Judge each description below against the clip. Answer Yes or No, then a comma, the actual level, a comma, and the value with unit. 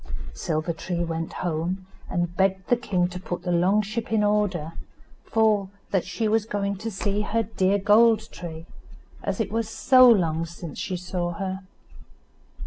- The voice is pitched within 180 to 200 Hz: Yes, high, 190 Hz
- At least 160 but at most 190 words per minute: Yes, average, 165 wpm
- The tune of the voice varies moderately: Yes, average, 3.4 semitones